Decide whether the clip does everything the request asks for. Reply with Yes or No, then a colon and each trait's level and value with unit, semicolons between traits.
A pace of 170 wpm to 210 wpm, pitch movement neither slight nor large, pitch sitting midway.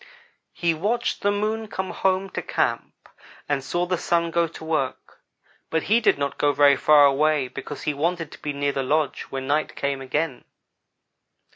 Yes: average, 180 wpm; average, 4.0 semitones; medium, 155 Hz